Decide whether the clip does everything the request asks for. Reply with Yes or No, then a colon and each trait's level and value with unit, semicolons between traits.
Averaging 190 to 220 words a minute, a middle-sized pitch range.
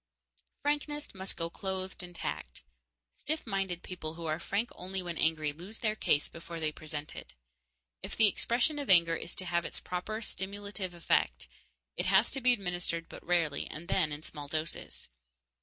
No: average, 175 wpm; average, 3.5 semitones